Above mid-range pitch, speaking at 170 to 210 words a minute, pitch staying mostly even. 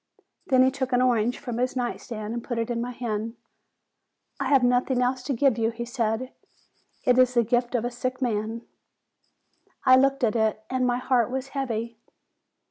Yes: high, 245 Hz; average, 195 wpm; narrow, 1.8 semitones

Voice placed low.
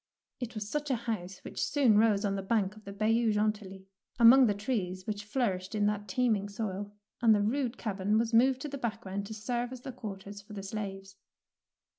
No: high, 215 Hz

